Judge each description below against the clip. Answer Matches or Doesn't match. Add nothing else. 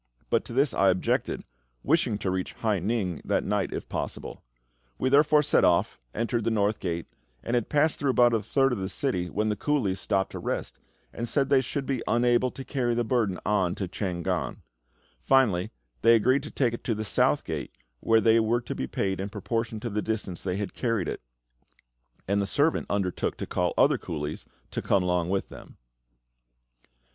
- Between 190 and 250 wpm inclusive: Matches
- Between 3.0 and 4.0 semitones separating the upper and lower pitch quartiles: Doesn't match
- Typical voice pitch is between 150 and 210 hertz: Doesn't match